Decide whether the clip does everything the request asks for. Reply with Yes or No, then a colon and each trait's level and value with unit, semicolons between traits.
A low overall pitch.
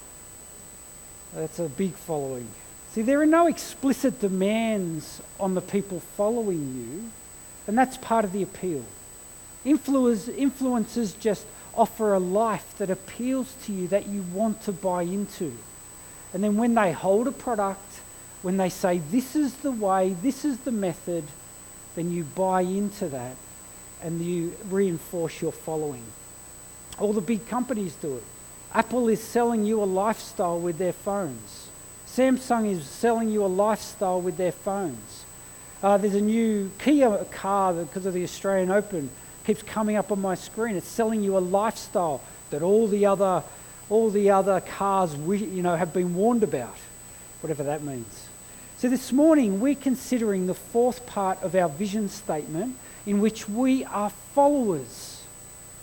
No: high, 195 Hz